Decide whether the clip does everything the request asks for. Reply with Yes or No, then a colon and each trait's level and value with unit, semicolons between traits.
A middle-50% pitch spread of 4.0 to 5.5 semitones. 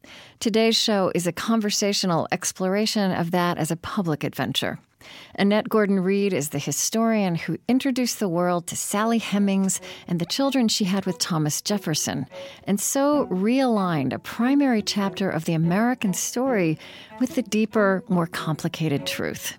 Yes: average, 4.4 semitones